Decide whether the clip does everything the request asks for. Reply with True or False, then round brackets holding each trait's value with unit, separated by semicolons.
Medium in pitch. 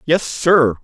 True (145 Hz)